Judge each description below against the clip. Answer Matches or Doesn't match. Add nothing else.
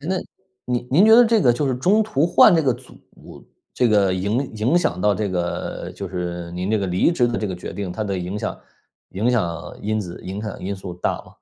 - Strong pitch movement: Matches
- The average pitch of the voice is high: Doesn't match